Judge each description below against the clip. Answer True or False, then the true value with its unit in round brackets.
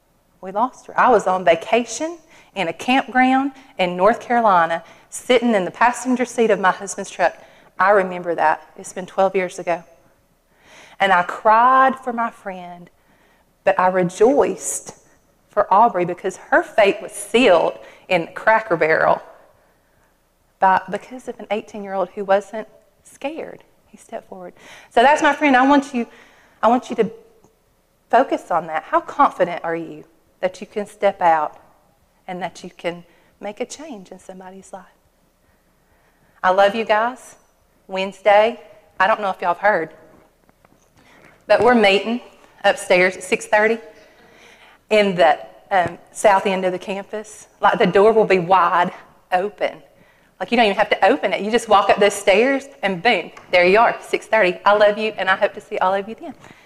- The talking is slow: False (175 wpm)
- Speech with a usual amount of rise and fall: True (3.7 semitones)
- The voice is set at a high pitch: True (200 Hz)